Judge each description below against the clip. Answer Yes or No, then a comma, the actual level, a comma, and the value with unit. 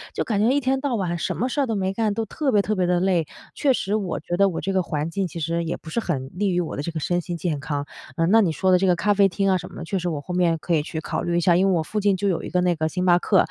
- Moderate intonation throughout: Yes, average, 3.1 semitones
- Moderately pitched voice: Yes, medium, 180 Hz